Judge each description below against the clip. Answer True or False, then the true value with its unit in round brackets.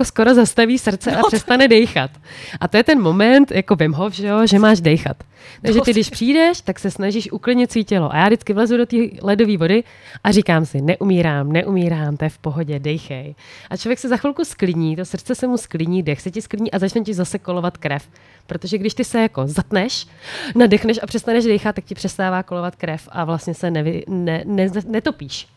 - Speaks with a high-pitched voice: True (195 Hz)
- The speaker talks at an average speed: False (210 wpm)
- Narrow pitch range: False (5.1 semitones)